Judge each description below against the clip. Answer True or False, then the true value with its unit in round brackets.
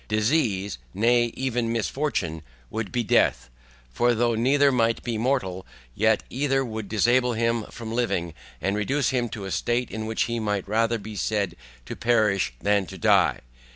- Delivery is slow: False (165 wpm)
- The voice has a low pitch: True (115 Hz)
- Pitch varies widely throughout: False (2.9 semitones)